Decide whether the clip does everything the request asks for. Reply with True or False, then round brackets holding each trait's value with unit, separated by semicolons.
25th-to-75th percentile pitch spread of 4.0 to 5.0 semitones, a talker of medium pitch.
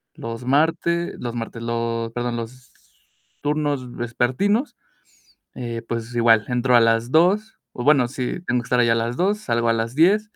False (4.3 semitones; 120 Hz)